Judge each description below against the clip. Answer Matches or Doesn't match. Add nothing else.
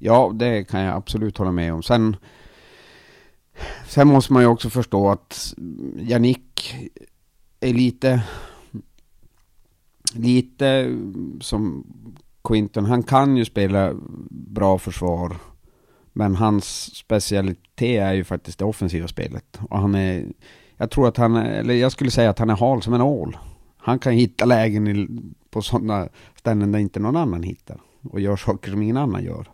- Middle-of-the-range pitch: Doesn't match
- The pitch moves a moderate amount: Matches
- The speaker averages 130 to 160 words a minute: Matches